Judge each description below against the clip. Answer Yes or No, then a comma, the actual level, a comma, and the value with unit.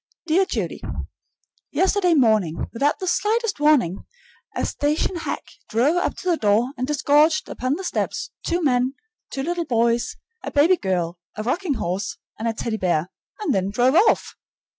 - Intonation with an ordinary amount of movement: No, wide, 7.6 semitones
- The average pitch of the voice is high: Yes, very high, 270 Hz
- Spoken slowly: No, average, 160 wpm